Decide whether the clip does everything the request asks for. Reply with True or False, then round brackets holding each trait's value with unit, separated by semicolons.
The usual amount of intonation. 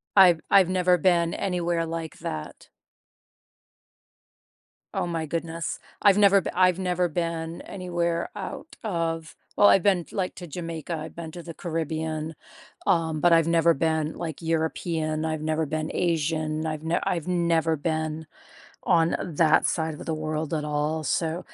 False (1.7 semitones)